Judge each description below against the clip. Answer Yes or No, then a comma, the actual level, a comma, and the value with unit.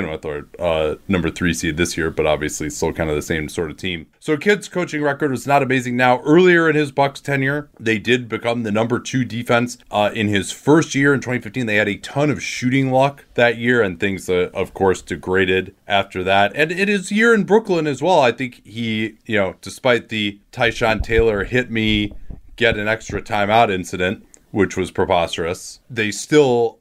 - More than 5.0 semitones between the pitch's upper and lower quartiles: Yes, wide, 5.5 semitones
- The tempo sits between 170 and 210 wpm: Yes, fast, 205 wpm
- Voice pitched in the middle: No, low, 115 Hz